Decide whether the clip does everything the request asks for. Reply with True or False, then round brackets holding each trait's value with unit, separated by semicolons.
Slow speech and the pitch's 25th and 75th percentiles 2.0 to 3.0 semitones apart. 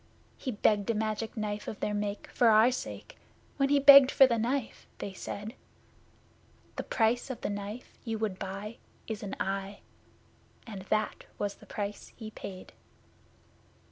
False (160 wpm; 2.4 semitones)